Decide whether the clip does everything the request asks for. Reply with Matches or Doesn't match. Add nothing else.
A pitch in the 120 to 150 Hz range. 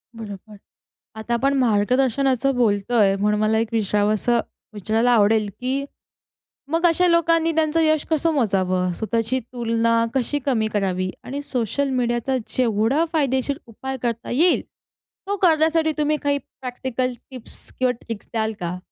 Doesn't match